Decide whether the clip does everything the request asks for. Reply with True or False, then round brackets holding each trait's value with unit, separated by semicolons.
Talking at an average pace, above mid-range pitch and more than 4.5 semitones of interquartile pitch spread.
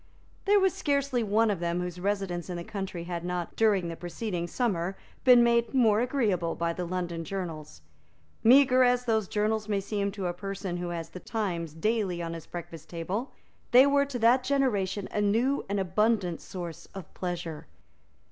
True (180 wpm; 195 Hz; 5.0 semitones)